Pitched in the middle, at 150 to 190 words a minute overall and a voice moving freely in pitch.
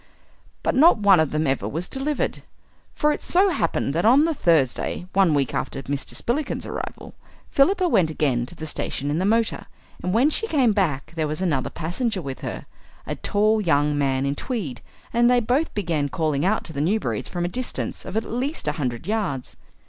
No: medium, 180 Hz; average, 200 wpm; wide, 8.5 semitones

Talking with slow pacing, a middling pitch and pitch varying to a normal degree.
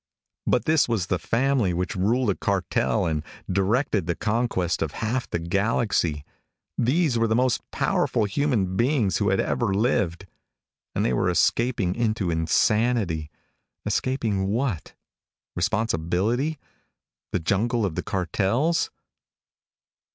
No: slow, 125 wpm; low, 105 Hz; average, 5.0 semitones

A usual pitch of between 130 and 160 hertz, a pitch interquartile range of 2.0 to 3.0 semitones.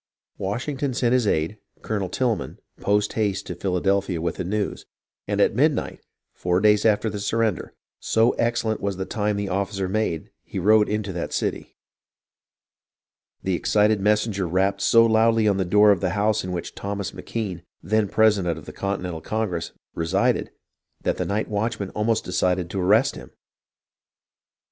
No: low, 100 Hz; average, 2.7 semitones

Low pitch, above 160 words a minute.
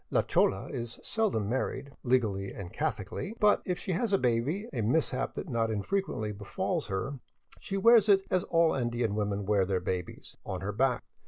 Yes: low, 120 Hz; average, 190 wpm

